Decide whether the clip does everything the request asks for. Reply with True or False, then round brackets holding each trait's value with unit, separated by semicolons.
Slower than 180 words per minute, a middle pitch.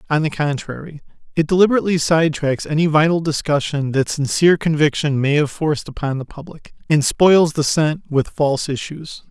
True (170 wpm; 155 Hz)